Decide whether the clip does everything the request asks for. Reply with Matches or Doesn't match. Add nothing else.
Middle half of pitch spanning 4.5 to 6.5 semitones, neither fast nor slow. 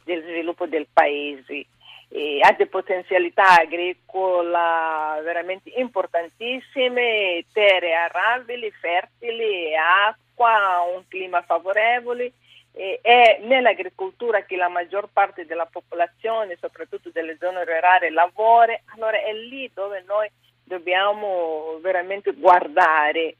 Doesn't match